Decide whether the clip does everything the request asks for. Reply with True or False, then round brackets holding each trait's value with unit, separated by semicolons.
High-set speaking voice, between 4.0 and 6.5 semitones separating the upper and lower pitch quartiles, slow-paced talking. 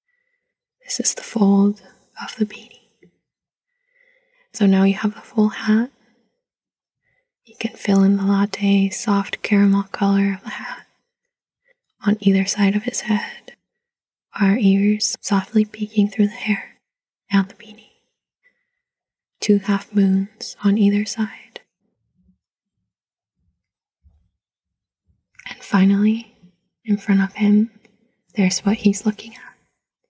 False (210 Hz; 2.9 semitones; 120 wpm)